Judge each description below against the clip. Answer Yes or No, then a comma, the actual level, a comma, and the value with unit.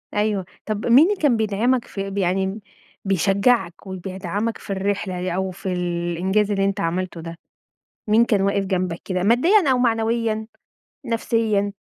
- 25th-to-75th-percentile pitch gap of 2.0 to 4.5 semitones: Yes, average, 3.3 semitones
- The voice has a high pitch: Yes, high, 200 Hz